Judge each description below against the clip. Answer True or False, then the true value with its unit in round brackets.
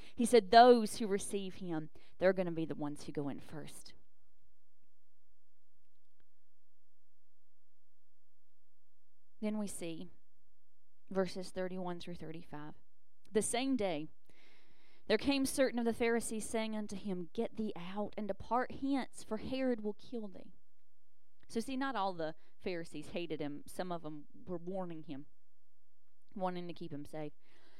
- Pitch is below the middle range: False (180 Hz)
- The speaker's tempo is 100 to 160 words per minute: True (140 wpm)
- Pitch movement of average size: False (6.8 semitones)